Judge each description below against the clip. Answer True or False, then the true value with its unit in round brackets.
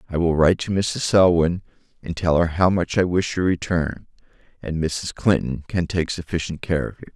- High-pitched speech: False (85 Hz)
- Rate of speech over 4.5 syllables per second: True (5.1 syllables/s)